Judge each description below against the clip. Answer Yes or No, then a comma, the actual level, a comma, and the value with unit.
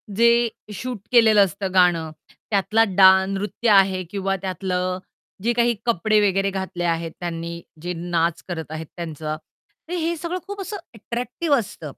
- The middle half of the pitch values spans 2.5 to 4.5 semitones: No, average, 5.3 semitones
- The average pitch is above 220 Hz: No, high, 195 Hz